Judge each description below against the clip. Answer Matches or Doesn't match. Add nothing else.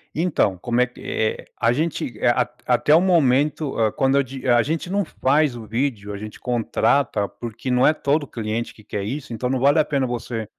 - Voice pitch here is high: Doesn't match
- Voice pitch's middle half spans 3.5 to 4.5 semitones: Matches